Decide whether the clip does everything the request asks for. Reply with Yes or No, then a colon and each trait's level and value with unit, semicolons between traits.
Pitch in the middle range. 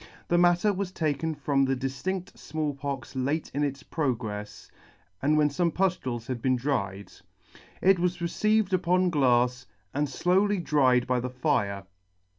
Yes: medium, 145 Hz